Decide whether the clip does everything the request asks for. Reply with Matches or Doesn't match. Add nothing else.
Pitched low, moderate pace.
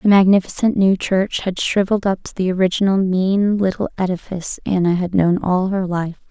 Doesn't match